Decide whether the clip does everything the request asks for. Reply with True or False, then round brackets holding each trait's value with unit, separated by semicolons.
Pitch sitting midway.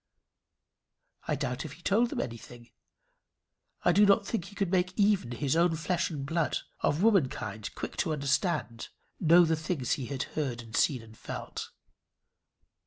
True (160 Hz)